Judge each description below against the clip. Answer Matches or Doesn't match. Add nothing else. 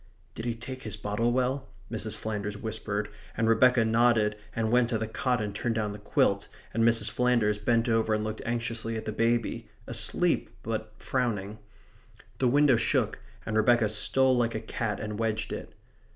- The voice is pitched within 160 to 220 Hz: Doesn't match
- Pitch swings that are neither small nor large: Doesn't match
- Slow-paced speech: Doesn't match